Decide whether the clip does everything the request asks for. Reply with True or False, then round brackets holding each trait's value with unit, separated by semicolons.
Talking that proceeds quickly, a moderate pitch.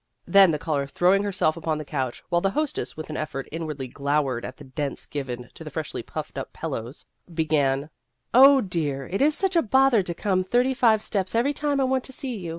True (230 wpm; 170 Hz)